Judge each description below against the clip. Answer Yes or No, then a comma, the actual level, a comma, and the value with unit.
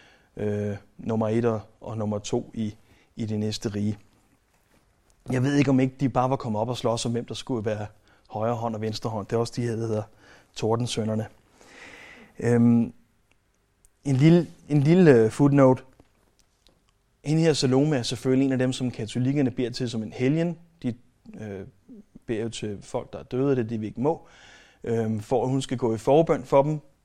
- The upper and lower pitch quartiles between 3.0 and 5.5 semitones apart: Yes, average, 3.5 semitones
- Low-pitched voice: Yes, low, 115 Hz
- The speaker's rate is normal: Yes, average, 195 wpm